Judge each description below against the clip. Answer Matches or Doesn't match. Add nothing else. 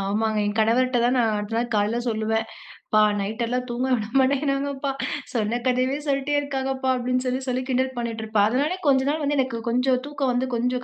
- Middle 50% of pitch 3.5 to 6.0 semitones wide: Doesn't match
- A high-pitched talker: Matches